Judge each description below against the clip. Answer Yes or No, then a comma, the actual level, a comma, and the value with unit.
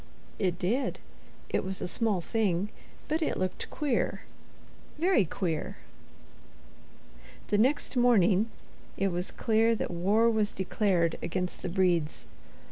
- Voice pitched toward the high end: Yes, high, 195 Hz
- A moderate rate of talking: No, slow, 125 wpm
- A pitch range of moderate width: Yes, average, 4.2 semitones